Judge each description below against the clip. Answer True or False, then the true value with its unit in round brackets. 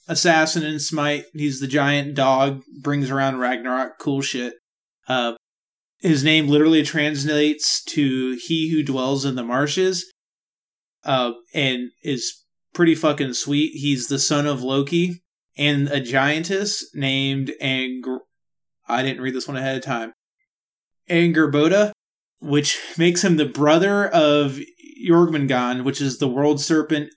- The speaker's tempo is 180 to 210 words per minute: False (135 wpm)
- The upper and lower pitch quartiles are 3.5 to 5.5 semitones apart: False (2.9 semitones)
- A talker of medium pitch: True (145 Hz)